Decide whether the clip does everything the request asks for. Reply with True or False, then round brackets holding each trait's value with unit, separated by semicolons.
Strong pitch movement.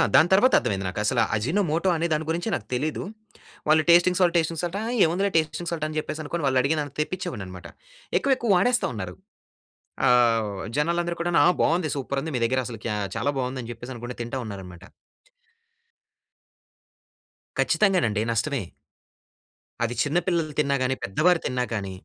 True (6.2 semitones)